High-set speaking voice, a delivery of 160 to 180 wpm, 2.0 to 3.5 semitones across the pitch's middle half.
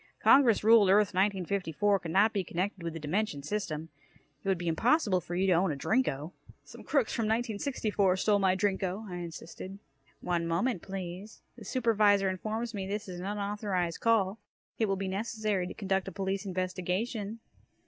Yes: high, 195 Hz; average, 175 wpm; average, 2.8 semitones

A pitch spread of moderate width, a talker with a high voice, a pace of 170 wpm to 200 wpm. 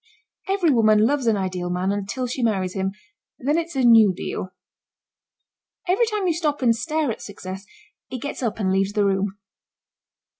No: wide, 6.9 semitones; high, 225 Hz; average, 175 wpm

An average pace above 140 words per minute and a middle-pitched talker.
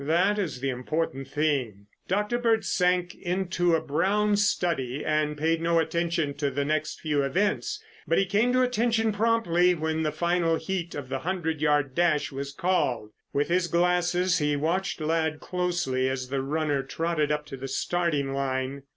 Yes: average, 170 wpm; medium, 160 Hz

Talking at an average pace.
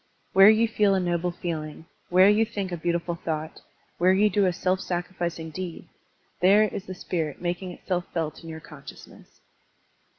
Yes: average, 175 wpm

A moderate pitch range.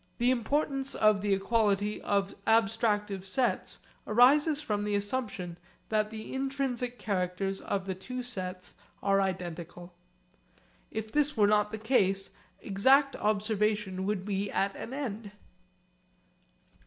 Yes: average, 3.9 semitones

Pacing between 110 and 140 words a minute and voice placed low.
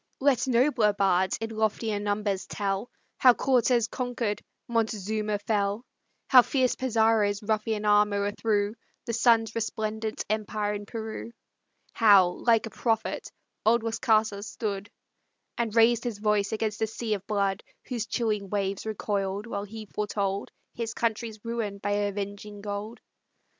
No: slow, 135 wpm; high, 215 Hz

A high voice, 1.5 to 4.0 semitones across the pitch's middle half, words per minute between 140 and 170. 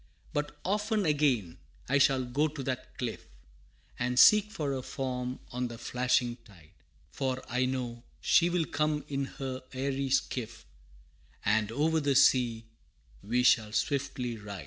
No: low, 130 Hz; average, 2.8 semitones; average, 145 wpm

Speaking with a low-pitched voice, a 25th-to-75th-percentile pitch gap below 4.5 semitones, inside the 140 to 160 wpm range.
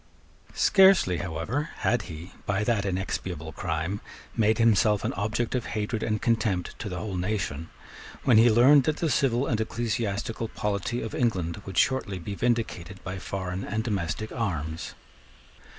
Yes: low, 105 Hz; average, 4.0 semitones; average, 150 wpm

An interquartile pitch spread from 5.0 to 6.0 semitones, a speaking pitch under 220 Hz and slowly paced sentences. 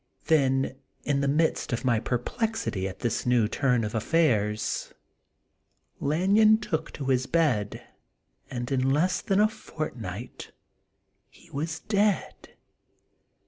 Yes: wide, 5.5 semitones; low, 135 Hz; slow, 130 wpm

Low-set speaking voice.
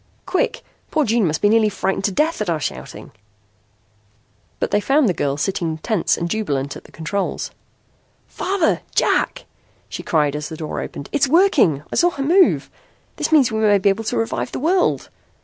No: high, 205 Hz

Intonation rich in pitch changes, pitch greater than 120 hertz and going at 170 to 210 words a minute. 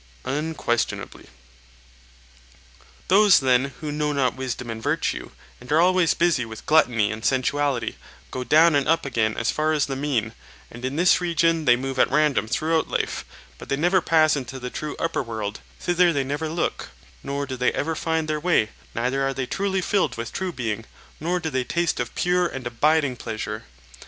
No: average, 4.6 semitones; medium, 140 Hz; average, 185 wpm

